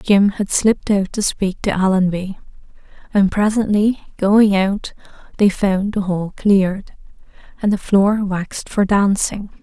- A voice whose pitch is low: No, high, 200 Hz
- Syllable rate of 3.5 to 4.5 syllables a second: Yes, 4.1 syllables/s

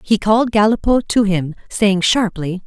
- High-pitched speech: Yes, high, 205 Hz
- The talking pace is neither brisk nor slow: Yes, average, 160 wpm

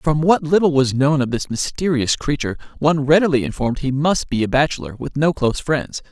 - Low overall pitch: No, medium, 145 Hz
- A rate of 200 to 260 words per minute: Yes, fast, 205 wpm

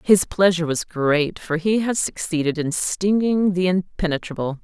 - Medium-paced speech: Yes, average, 155 wpm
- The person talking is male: No, female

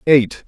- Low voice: Yes, low, 125 Hz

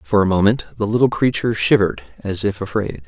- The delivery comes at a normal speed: Yes, average, 195 wpm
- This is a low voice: Yes, low, 105 Hz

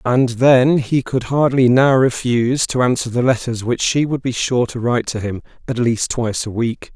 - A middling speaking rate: No, fast, 215 wpm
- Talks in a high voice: No, low, 125 Hz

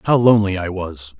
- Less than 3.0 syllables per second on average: No, 5.8 syllables/s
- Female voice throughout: No, male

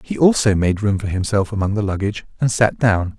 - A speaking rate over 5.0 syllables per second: Yes, 5.7 syllables/s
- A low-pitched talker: Yes, low, 105 Hz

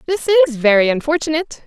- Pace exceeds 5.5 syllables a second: Yes, 7.1 syllables/s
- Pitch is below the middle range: No, very high, 295 Hz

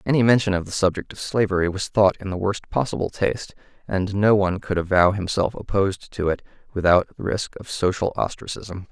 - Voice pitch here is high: No, low, 100 Hz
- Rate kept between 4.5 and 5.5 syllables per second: No, 5.7 syllables/s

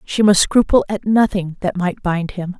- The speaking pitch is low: No, high, 190 Hz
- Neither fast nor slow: No, fast, 210 wpm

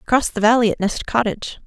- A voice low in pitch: No, high, 225 Hz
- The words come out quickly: Yes, fast, 215 wpm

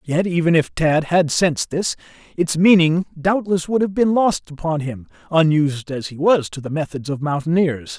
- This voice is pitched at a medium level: Yes, medium, 165 Hz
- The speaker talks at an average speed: Yes, average, 190 wpm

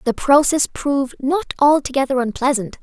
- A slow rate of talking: Yes, slow, 125 wpm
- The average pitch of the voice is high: Yes, very high, 270 Hz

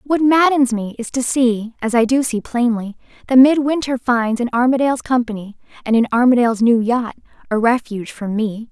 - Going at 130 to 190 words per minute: Yes, average, 180 wpm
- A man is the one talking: No, female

